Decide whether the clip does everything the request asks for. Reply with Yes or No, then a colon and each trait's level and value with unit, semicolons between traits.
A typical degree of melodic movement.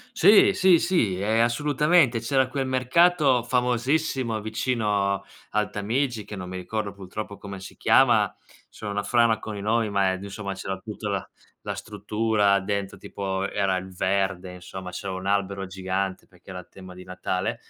Yes: average, 3.9 semitones